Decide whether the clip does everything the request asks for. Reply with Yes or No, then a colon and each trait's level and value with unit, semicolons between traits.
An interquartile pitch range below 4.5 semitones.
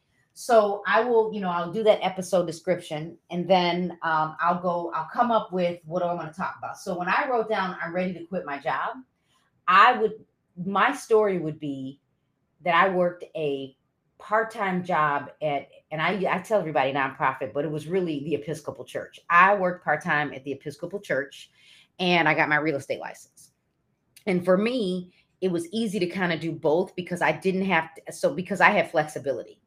Yes: average, 3.6 semitones